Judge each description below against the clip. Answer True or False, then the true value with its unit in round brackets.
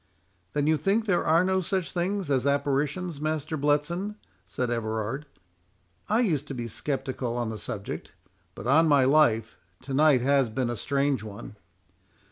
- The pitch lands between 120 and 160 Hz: True (140 Hz)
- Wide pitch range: False (4.3 semitones)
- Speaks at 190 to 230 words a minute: False (160 wpm)